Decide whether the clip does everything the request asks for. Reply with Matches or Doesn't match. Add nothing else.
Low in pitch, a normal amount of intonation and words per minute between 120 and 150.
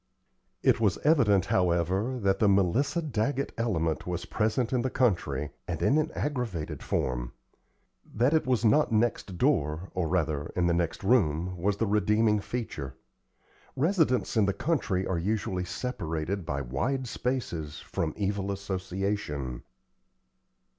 Doesn't match